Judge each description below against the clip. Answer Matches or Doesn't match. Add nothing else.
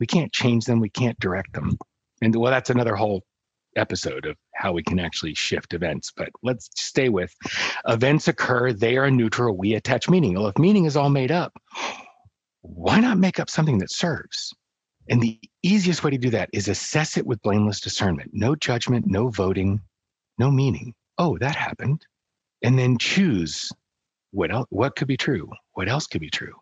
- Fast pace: Doesn't match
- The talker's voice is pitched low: Matches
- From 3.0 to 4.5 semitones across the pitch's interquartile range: Doesn't match